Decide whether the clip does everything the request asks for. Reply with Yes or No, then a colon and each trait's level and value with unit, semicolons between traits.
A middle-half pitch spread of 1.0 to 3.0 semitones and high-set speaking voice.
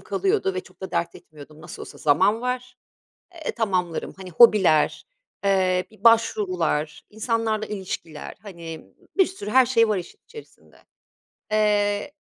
No: average, 4.2 semitones; high, 205 Hz